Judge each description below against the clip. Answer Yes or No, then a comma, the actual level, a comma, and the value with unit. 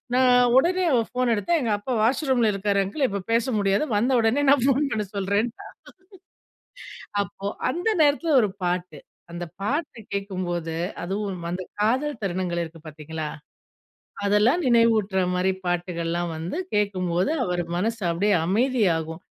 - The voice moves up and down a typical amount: No, wide, 5.7 semitones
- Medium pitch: No, high, 200 Hz